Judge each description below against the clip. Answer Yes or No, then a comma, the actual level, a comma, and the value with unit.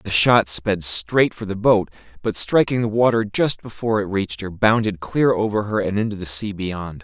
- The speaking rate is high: Yes, fast, 215 wpm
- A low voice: Yes, low, 105 Hz